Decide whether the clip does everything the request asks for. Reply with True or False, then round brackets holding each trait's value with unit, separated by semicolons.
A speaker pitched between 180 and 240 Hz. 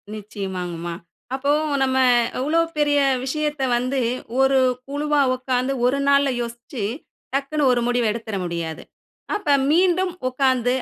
False (265 Hz)